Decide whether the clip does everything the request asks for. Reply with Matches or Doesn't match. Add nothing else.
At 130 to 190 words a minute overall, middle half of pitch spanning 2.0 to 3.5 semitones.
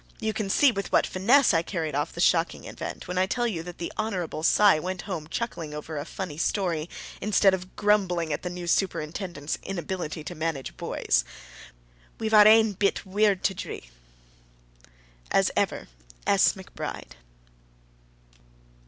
Doesn't match